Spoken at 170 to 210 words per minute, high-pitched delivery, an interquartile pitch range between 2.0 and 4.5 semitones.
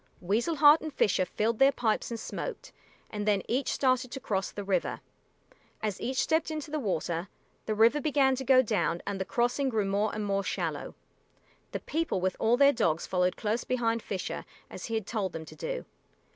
No: average, 200 wpm; high, 225 Hz; average, 5.3 semitones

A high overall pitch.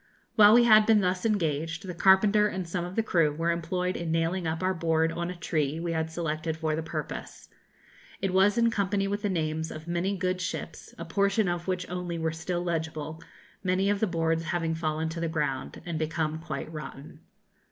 No: medium, 170 Hz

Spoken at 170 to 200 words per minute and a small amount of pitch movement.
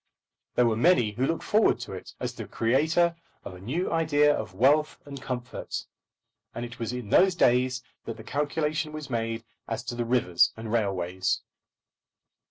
No: average, 175 wpm; average, 4.9 semitones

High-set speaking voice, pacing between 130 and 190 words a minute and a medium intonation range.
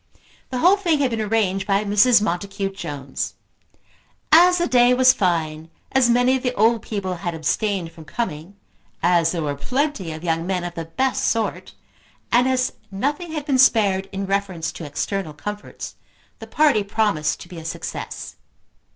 No: high, 200 Hz; average, 170 wpm; wide, 6.6 semitones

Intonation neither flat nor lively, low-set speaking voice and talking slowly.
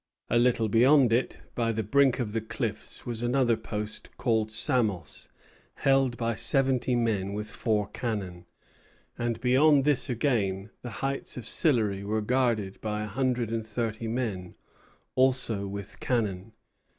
No: average, 3.1 semitones; low, 115 Hz; average, 145 wpm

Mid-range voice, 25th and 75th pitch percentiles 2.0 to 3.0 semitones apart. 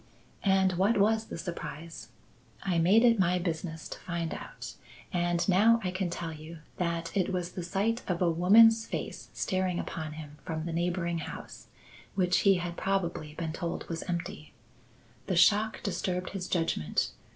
Yes: medium, 180 Hz; narrow, 2.5 semitones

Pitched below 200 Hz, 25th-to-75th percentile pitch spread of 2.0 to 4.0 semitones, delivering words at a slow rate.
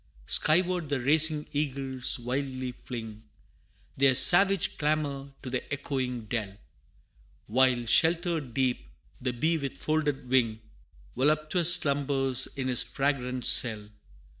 Yes: low, 135 Hz; average, 3.5 semitones; slow, 115 wpm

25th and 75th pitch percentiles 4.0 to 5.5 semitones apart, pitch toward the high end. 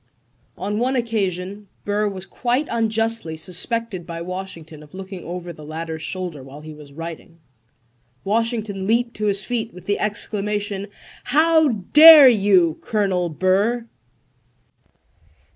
Yes: average, 4.6 semitones; high, 200 Hz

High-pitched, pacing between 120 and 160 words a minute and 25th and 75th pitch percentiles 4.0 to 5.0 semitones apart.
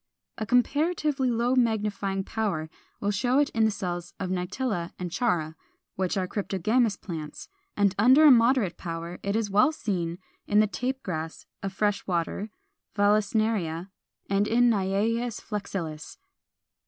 Yes: high, 205 Hz; average, 145 wpm; average, 4.3 semitones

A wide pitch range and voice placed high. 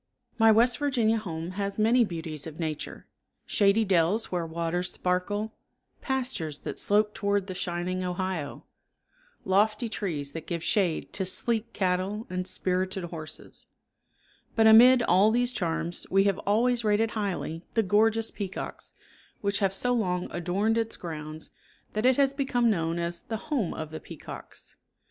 No: average, 4.3 semitones; high, 195 Hz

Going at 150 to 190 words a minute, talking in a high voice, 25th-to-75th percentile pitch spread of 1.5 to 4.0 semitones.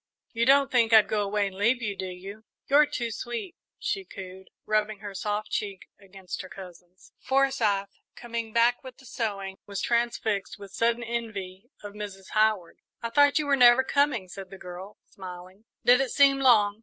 Yes: average, 180 wpm; high, 215 Hz; average, 3.7 semitones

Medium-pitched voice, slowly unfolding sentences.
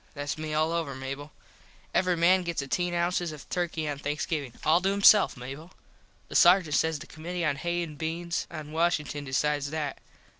No: medium, 160 Hz; average, 180 wpm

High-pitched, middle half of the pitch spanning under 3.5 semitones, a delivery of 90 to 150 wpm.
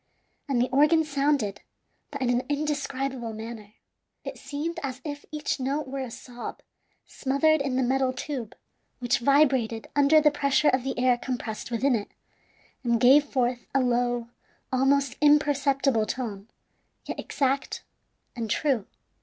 Yes: very high, 265 Hz; average, 2.9 semitones; average, 145 wpm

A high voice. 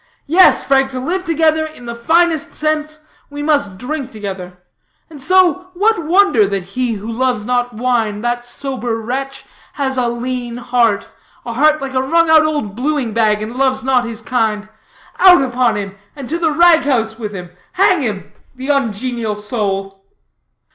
Yes: very high, 255 Hz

